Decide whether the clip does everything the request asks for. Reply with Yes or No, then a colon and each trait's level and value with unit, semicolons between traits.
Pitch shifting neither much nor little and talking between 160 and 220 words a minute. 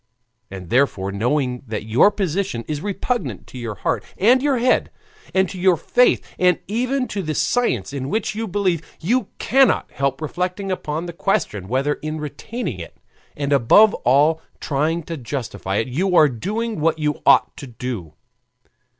No: wide, 7.7 semitones; average, 165 wpm